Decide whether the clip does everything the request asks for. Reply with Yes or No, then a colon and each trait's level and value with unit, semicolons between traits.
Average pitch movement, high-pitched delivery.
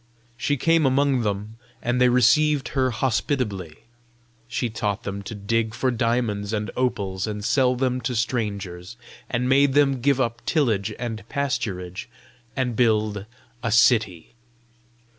No: average, 3.8 semitones; low, 115 Hz